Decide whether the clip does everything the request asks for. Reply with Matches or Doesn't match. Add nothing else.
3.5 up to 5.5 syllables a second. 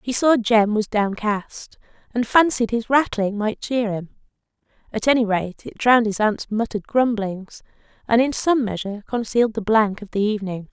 Matches